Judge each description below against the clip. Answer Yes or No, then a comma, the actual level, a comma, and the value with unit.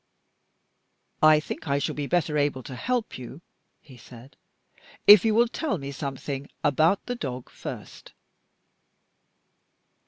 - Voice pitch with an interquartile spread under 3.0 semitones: No, average, 4.9 semitones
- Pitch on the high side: No, medium, 145 Hz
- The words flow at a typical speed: No, slow, 130 wpm